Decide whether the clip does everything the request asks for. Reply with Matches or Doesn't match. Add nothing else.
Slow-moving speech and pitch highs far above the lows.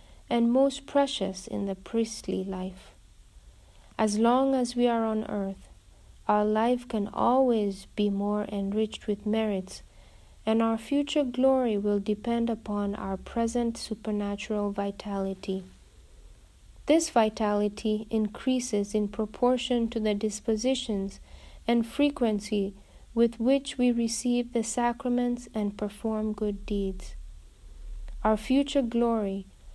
Doesn't match